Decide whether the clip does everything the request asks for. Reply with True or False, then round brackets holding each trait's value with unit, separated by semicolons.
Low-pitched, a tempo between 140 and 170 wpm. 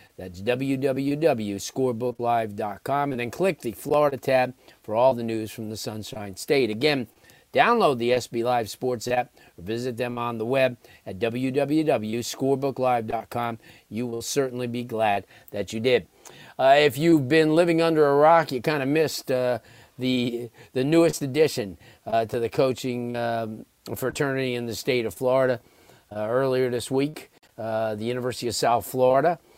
True (125 Hz; 155 wpm)